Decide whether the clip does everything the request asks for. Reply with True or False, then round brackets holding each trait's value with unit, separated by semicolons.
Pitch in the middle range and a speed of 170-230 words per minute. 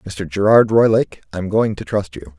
False (100 Hz; 200 wpm)